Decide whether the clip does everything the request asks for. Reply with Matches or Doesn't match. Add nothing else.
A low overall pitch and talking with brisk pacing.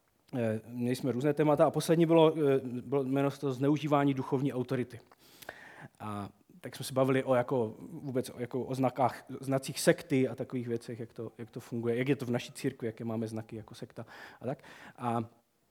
Matches